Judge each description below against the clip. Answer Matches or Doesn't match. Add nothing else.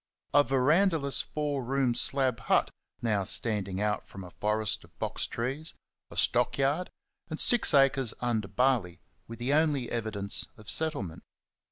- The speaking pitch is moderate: Doesn't match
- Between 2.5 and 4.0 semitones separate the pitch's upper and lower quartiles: Doesn't match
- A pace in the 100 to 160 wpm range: Matches